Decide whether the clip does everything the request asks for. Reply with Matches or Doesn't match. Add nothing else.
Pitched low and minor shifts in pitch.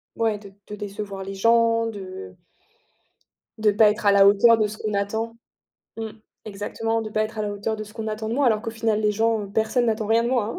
Doesn't match